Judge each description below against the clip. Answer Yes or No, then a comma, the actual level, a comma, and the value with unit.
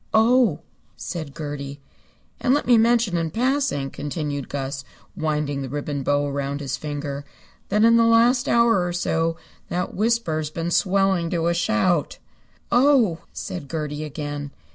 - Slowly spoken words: No, average, 150 wpm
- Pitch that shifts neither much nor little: No, wide, 7.4 semitones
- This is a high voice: No, medium, 165 Hz